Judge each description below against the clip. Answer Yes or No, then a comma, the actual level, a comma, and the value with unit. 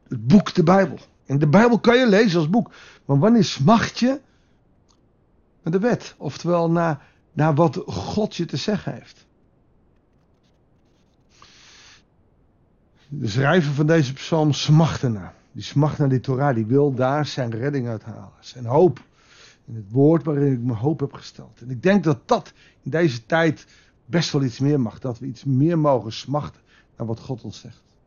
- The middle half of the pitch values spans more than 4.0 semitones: Yes, average, 4.7 semitones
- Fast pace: No, average, 175 wpm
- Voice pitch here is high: No, medium, 140 Hz